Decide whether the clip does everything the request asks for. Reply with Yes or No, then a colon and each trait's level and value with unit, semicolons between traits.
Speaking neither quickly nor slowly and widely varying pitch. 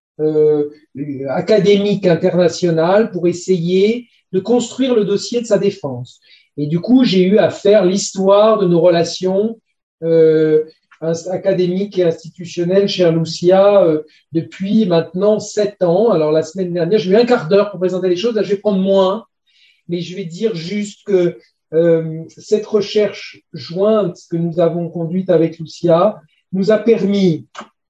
No: average, 155 wpm; average, 3.5 semitones